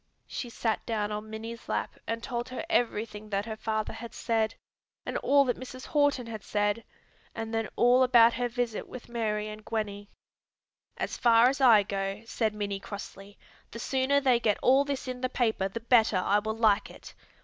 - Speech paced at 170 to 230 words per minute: Yes, average, 190 wpm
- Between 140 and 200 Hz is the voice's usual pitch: No, high, 225 Hz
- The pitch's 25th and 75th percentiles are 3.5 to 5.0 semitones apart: No, narrow, 2.6 semitones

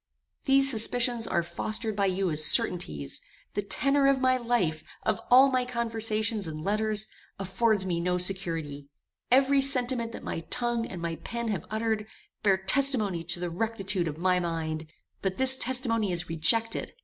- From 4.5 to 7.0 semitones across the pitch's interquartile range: Yes, wide, 5.4 semitones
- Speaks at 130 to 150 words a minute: No, average, 160 wpm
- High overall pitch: Yes, high, 210 Hz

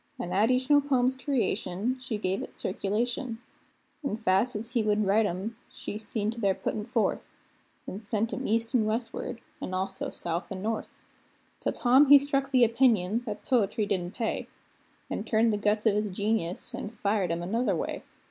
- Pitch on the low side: No, high, 220 Hz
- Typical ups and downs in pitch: Yes, average, 3.4 semitones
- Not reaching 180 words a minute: No, average, 185 wpm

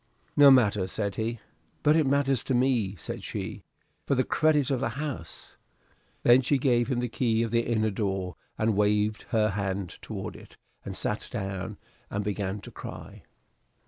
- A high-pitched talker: No, low, 110 Hz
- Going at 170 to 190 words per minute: Yes, average, 175 wpm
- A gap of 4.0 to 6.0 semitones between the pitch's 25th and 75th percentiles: Yes, average, 4.4 semitones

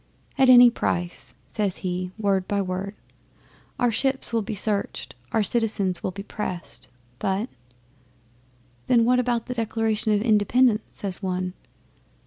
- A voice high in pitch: Yes, high, 210 Hz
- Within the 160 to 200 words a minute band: No, average, 140 wpm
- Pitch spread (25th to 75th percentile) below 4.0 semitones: Yes, average, 3.6 semitones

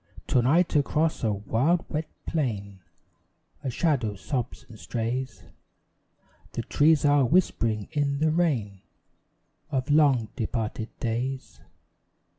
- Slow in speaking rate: Yes, slow, 110 wpm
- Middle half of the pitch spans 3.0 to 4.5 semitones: No, average, 5.1 semitones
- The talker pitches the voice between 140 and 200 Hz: No, low, 130 Hz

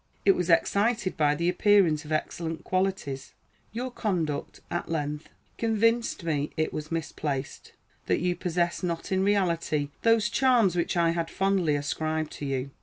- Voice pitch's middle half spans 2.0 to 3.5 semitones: No, average, 4.2 semitones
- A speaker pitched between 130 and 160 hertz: No, medium, 170 Hz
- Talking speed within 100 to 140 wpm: No, average, 155 wpm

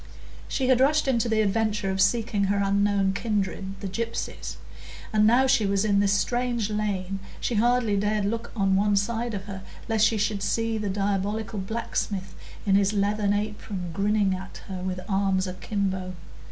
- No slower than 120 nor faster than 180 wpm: Yes, average, 170 wpm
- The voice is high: Yes, high, 205 Hz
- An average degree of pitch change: No, narrow, 2.2 semitones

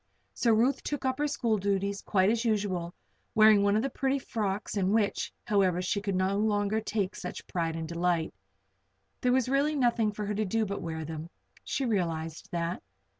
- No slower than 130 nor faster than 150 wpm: No, average, 190 wpm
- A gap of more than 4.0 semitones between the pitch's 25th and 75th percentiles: No, average, 3.7 semitones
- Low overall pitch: No, high, 205 Hz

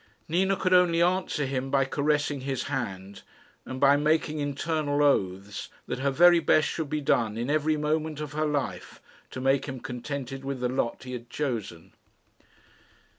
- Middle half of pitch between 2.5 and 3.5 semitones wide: Yes, average, 3.1 semitones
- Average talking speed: Yes, average, 170 wpm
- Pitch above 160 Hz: No, medium, 140 Hz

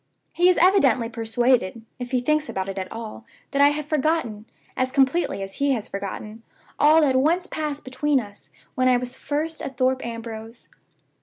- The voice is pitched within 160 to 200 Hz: No, very high, 255 Hz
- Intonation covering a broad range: No, average, 4.7 semitones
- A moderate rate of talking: Yes, average, 180 wpm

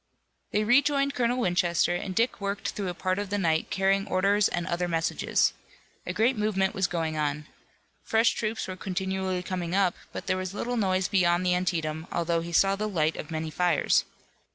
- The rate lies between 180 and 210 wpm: Yes, average, 190 wpm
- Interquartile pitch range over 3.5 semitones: No, average, 2.9 semitones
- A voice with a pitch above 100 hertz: Yes, medium, 185 Hz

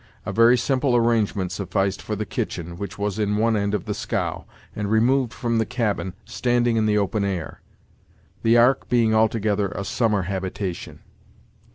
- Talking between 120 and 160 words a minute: No, average, 170 wpm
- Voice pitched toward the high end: No, low, 105 Hz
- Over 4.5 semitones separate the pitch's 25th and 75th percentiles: No, average, 2.8 semitones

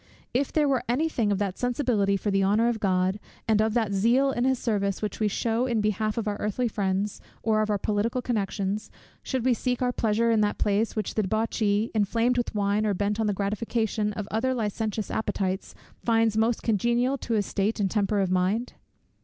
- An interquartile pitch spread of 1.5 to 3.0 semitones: Yes, narrow, 2.5 semitones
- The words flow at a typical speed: No, fast, 210 wpm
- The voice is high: Yes, high, 215 Hz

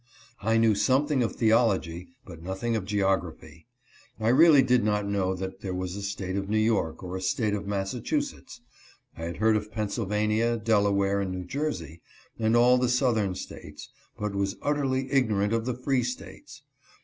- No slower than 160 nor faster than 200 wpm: Yes, average, 175 wpm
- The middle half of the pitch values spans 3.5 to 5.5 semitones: Yes, average, 3.8 semitones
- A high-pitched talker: No, low, 105 Hz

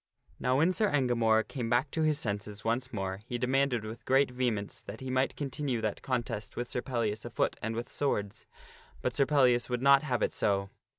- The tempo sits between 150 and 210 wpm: Yes, average, 200 wpm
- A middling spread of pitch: Yes, average, 3.4 semitones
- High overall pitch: No, low, 125 Hz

